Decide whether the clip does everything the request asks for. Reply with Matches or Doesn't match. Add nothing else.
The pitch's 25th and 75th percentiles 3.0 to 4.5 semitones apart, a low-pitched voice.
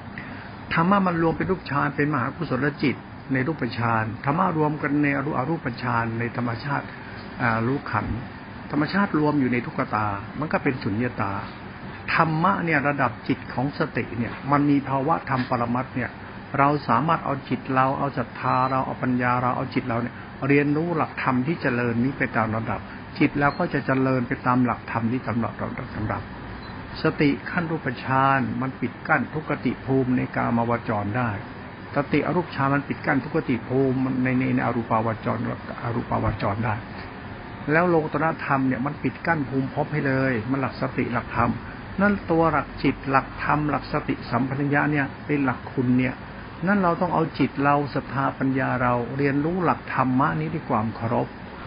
Matches